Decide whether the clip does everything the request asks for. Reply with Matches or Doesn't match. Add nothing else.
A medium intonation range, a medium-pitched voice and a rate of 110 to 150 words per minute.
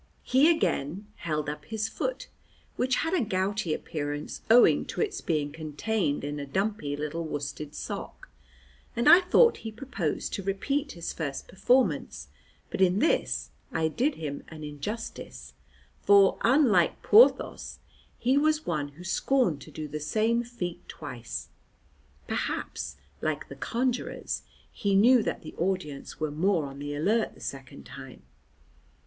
Doesn't match